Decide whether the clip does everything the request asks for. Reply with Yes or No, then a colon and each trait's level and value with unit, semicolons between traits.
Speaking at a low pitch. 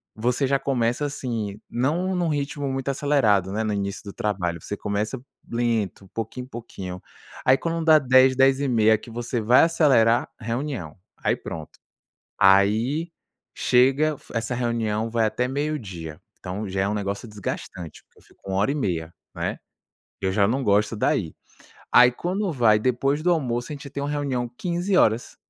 Yes: low, 120 Hz